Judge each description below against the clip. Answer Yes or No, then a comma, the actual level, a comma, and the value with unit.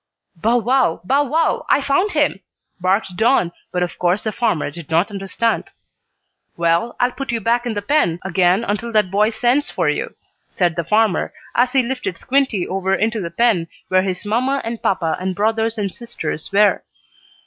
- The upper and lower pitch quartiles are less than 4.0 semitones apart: No, average, 4.7 semitones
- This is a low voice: No, high, 210 Hz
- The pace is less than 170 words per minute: No, average, 180 wpm